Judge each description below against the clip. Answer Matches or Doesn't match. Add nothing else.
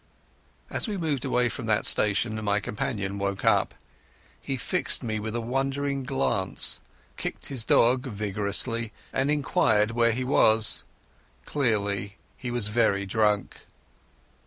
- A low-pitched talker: Matches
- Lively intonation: Doesn't match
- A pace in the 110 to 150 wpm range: Matches